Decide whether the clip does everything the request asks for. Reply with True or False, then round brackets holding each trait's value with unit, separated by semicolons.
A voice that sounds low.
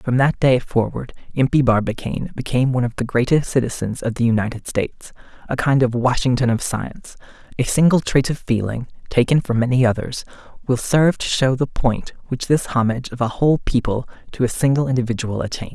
True (125 Hz)